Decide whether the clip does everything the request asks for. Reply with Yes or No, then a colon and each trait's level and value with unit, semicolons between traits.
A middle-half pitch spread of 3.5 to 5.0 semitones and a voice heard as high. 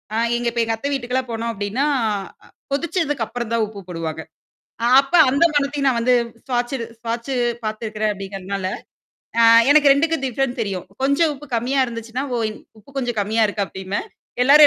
Yes: average, 4.3 semitones; high, 240 Hz